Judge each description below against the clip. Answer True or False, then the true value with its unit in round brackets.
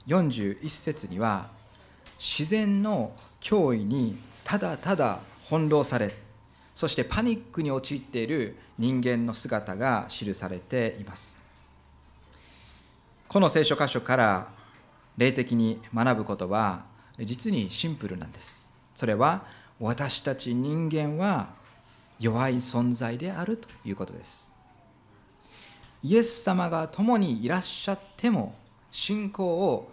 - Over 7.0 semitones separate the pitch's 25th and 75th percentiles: True (7.4 semitones)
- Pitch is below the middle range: True (125 Hz)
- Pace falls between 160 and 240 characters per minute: True (220 characters per minute)